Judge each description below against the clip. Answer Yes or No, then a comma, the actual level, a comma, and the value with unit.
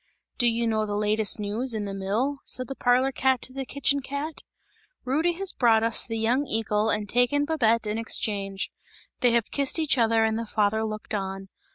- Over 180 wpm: Yes, average, 200 wpm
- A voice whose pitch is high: Yes, high, 230 Hz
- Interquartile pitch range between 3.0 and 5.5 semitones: Yes, average, 3.7 semitones